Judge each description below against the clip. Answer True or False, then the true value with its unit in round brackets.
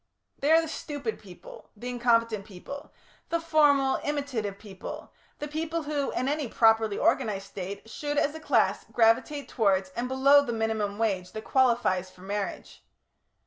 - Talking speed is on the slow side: False (155 wpm)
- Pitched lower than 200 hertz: False (235 Hz)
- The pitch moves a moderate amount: False (5.8 semitones)